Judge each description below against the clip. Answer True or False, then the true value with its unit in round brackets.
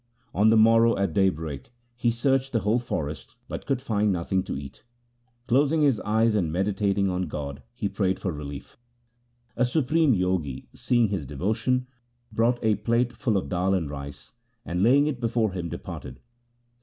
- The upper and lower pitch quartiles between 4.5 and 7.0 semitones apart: True (5.1 semitones)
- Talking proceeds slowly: False (185 wpm)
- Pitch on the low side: True (105 Hz)